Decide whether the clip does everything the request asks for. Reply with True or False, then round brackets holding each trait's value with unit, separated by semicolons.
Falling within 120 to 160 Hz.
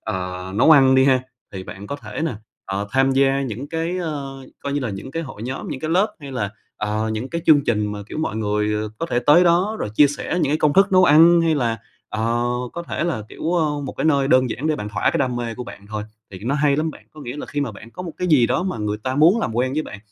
True (135 Hz)